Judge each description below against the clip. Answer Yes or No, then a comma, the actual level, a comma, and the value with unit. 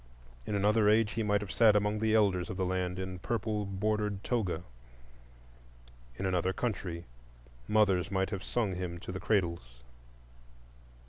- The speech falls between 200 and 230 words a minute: No, average, 150 wpm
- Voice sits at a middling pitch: No, low, 100 Hz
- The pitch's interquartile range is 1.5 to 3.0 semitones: Yes, narrow, 2.6 semitones